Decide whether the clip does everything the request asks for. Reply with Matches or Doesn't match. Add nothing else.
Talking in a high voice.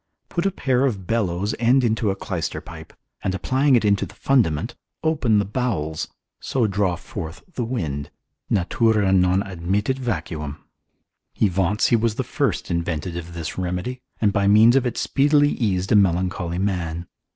Doesn't match